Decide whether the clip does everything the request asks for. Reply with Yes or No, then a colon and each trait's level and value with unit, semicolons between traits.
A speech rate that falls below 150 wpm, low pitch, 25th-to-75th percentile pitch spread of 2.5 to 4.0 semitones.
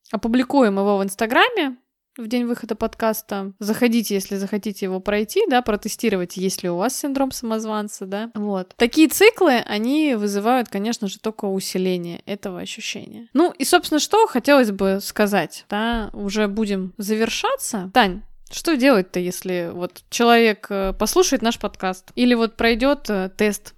No: average, 140 wpm; high, 220 Hz; average, 3.7 semitones